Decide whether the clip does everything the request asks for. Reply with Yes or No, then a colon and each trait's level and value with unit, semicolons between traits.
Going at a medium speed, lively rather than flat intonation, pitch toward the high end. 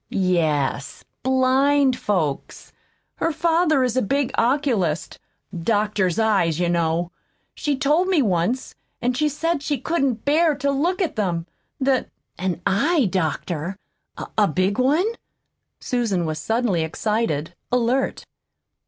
No: slow, 125 wpm; wide, 8.0 semitones; high, 230 Hz